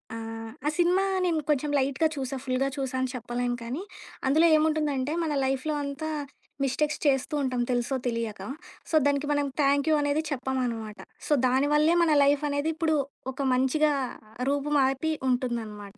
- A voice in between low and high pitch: No, very high, 275 Hz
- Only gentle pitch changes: No, average, 3.0 semitones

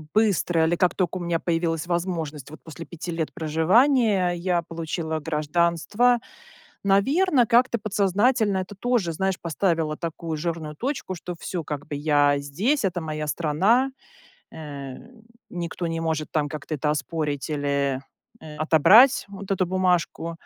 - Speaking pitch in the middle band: Yes, medium, 170 Hz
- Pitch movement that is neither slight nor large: Yes, average, 3.9 semitones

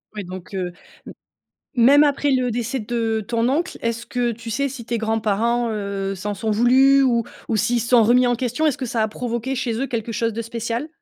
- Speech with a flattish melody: Yes, narrow, 2.2 semitones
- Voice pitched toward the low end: No, high, 235 Hz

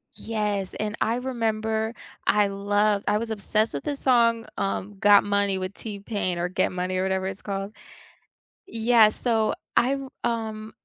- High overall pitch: Yes, high, 210 Hz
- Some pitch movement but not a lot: No, narrow, 2.3 semitones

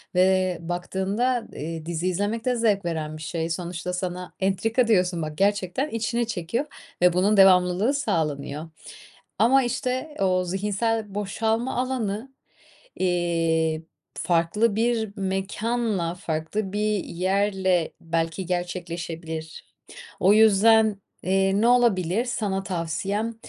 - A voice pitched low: No, high, 190 Hz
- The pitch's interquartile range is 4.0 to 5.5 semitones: Yes, average, 4.3 semitones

